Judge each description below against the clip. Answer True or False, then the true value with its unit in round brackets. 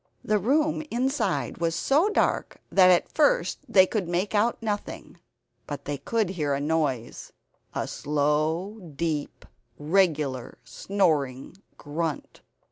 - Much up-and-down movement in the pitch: True (6.1 semitones)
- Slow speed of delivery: True (125 wpm)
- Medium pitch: True (170 Hz)